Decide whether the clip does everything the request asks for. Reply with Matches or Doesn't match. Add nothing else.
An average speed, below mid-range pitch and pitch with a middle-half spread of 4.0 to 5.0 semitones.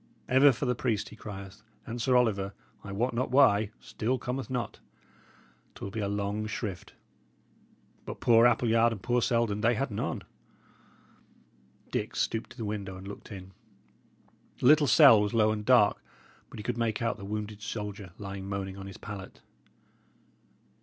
Doesn't match